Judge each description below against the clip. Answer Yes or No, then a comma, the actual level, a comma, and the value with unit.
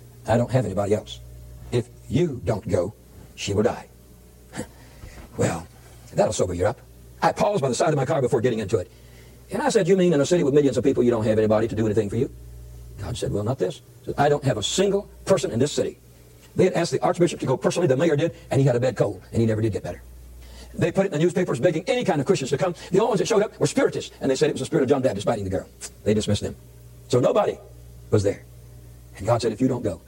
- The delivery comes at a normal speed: No, fast, 270 wpm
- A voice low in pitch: Yes, low, 115 Hz